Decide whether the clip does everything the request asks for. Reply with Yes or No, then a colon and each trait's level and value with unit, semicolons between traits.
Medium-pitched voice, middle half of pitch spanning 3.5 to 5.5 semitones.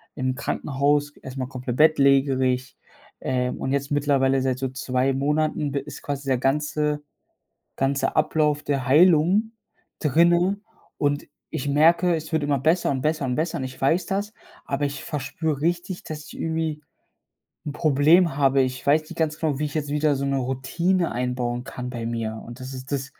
No: medium, 145 Hz; average, 2.8 semitones